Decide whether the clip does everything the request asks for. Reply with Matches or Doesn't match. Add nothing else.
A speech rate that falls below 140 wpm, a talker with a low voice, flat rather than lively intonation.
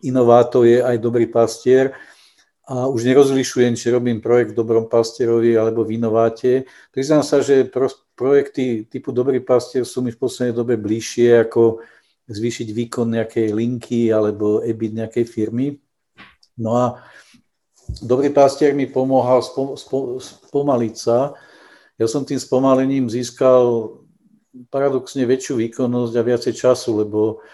Matches